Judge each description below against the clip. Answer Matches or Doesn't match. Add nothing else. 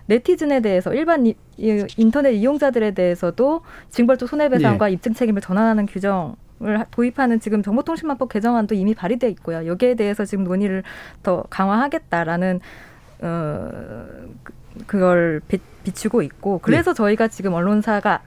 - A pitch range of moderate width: Matches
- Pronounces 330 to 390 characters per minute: Matches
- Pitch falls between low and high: Doesn't match